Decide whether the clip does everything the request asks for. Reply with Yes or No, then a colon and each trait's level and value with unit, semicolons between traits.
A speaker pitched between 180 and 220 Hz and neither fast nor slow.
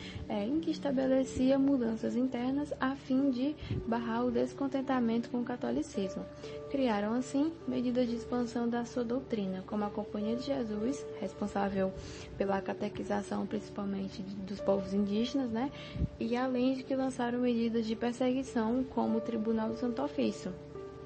No: high, 235 Hz; average, 140 wpm